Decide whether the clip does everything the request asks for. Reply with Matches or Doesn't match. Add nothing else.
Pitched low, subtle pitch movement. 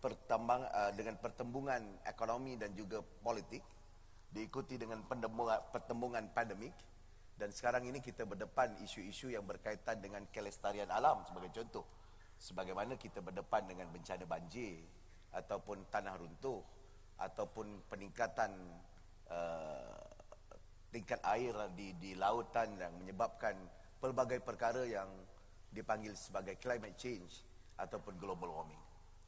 Doesn't match